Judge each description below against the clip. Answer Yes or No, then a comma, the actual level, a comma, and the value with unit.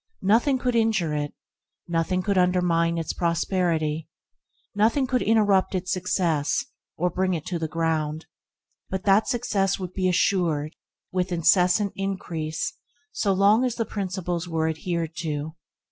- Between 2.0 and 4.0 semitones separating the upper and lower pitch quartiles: Yes, average, 3.2 semitones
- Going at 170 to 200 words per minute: No, average, 140 wpm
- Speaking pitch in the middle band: Yes, medium, 180 Hz